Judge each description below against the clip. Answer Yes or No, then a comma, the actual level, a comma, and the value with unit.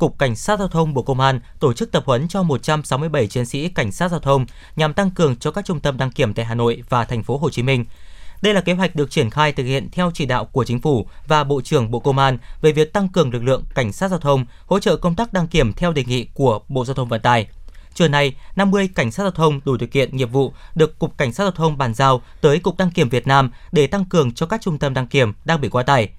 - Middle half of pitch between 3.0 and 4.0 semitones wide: No, average, 4.8 semitones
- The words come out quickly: Yes, fast, 280 wpm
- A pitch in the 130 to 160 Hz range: Yes, medium, 140 Hz